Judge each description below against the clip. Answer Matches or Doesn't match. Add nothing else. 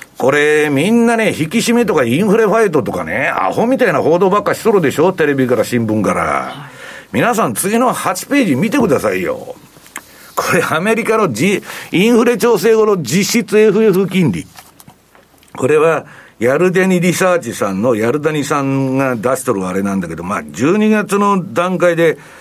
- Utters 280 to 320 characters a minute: Doesn't match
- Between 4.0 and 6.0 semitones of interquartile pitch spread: Doesn't match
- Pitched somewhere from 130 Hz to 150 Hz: Doesn't match